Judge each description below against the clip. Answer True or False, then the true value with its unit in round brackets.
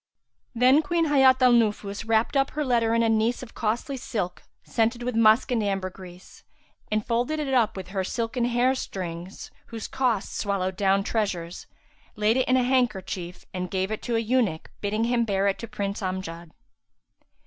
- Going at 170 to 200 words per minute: True (180 wpm)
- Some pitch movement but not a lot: True (4.2 semitones)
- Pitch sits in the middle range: False (225 Hz)